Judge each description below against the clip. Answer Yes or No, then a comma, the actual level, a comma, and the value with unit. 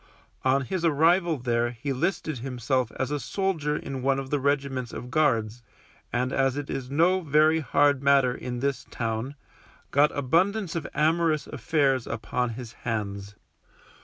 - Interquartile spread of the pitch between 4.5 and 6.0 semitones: No, average, 3.6 semitones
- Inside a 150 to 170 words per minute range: Yes, average, 155 wpm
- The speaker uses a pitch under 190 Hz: Yes, low, 135 Hz